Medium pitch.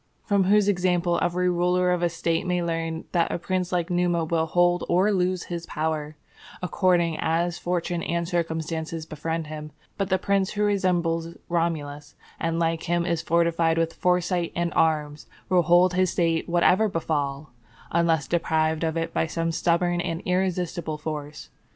Yes: medium, 170 Hz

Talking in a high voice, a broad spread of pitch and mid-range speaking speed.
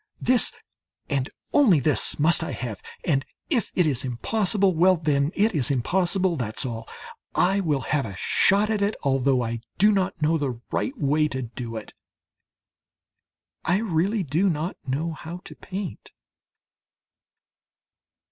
No: medium, 160 Hz; wide, 6.2 semitones; average, 145 wpm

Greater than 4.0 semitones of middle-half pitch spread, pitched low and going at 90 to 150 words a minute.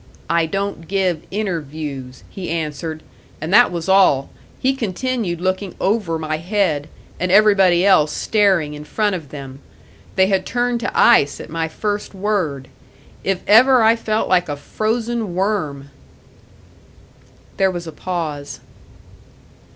No: average, 4.9 semitones; medium, 185 Hz; slow, 135 wpm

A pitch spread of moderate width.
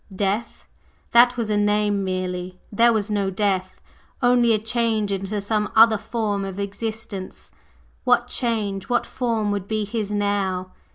No: narrow, 2.3 semitones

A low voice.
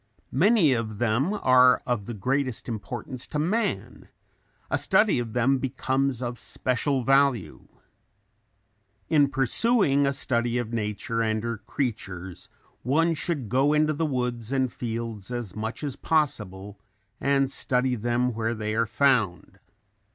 Yes: low, 125 Hz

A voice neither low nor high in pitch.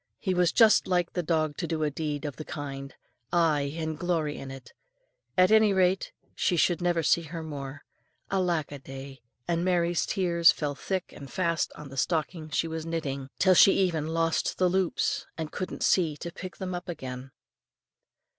Yes: medium, 165 Hz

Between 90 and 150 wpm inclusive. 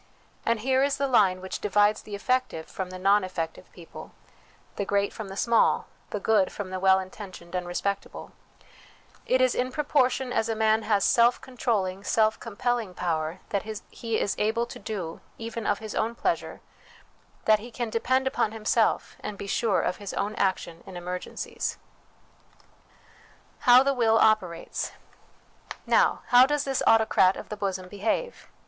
No: average, 165 wpm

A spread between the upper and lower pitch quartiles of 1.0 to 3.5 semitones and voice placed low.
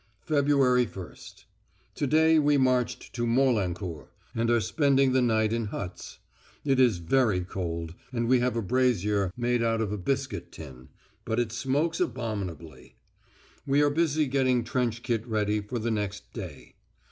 No: average, 4.3 semitones; low, 115 Hz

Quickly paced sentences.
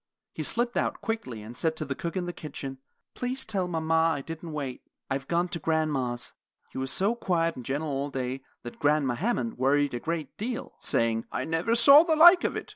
Yes: fast, 210 wpm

